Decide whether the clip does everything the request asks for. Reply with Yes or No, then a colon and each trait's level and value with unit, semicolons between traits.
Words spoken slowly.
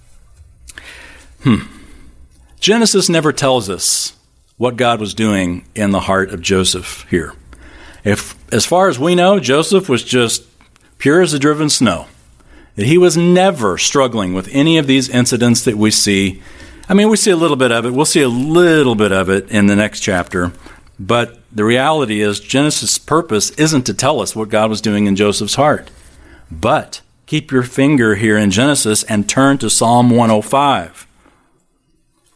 No: average, 165 wpm